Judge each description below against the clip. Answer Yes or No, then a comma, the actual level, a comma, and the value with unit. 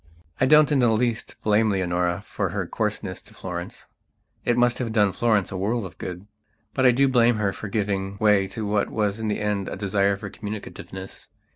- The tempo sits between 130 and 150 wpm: No, fast, 205 wpm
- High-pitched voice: No, low, 105 Hz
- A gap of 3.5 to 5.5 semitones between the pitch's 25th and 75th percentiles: No, average, 3.0 semitones